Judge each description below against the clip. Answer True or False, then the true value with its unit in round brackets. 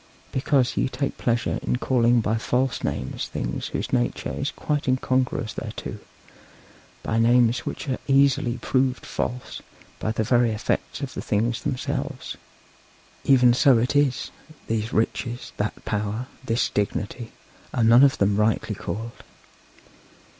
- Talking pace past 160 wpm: False (140 wpm)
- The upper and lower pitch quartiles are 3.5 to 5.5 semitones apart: False (2.5 semitones)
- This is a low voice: True (120 Hz)